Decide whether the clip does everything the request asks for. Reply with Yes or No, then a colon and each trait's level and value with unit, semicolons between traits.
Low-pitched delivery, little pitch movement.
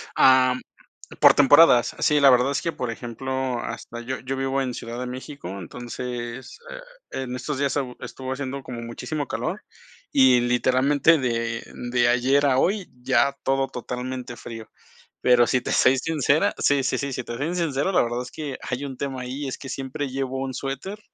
Yes: low, 130 Hz; narrow, 2.1 semitones